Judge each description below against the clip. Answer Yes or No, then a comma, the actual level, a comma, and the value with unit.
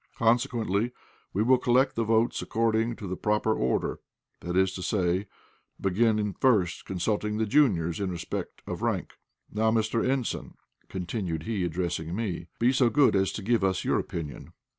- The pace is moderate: Yes, average, 160 wpm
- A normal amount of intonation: Yes, average, 3.9 semitones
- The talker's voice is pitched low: Yes, low, 105 Hz